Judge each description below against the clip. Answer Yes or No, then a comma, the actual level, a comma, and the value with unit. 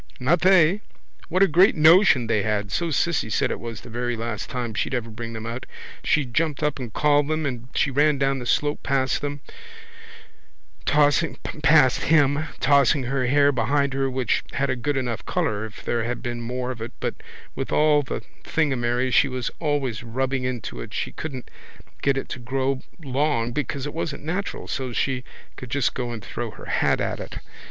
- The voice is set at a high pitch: No, low, 135 Hz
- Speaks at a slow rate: No, average, 190 wpm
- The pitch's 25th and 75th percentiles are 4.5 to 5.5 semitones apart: No, average, 3.4 semitones